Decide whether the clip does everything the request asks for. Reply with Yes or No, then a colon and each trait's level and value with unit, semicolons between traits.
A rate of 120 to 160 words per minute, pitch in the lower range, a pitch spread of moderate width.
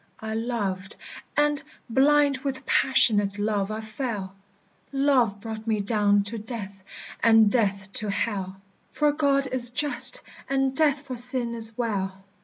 No: average, 140 wpm; high, 225 Hz; average, 4.6 semitones